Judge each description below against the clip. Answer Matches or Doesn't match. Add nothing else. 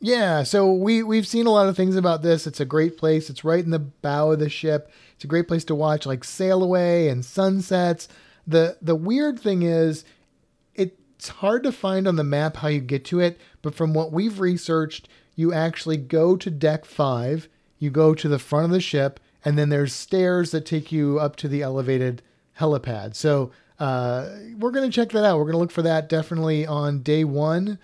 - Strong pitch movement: Doesn't match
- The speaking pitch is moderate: Matches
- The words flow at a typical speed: Doesn't match